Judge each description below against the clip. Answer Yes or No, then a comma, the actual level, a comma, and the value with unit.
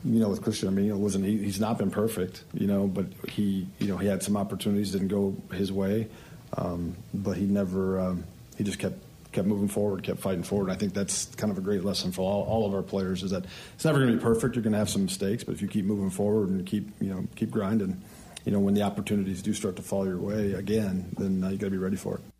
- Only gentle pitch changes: Yes, narrow, 1.4 semitones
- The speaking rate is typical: No, fast, 275 wpm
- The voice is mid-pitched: No, low, 100 Hz